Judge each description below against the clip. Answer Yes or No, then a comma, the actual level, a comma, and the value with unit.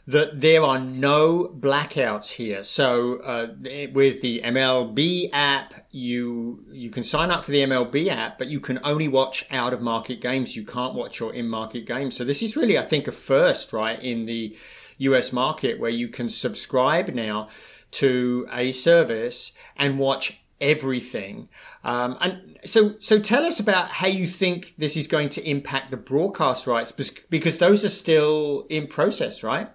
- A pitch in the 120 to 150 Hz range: Yes, low, 135 Hz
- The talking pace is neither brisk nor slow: Yes, average, 175 wpm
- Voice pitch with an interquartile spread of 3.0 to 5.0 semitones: Yes, average, 4.1 semitones